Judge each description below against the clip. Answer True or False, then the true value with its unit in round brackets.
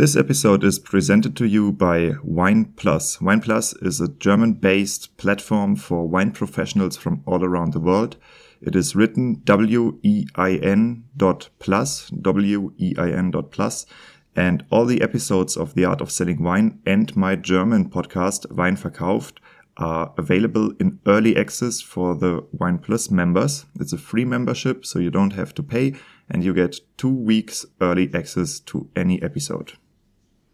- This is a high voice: False (100 Hz)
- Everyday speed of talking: True (165 wpm)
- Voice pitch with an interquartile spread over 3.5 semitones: True (4.4 semitones)